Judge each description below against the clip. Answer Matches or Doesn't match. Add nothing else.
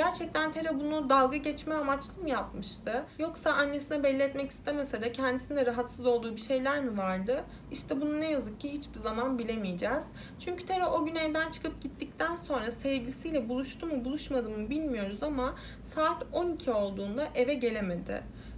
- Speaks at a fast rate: Matches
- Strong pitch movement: Doesn't match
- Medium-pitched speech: Doesn't match